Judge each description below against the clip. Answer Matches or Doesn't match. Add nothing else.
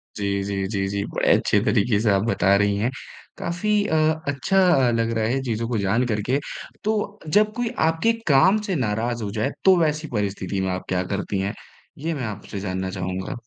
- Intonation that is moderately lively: Doesn't match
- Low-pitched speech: Matches